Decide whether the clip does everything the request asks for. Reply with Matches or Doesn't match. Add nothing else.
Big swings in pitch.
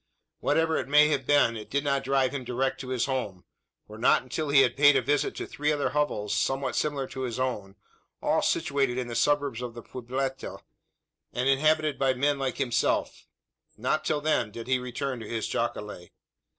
Doesn't match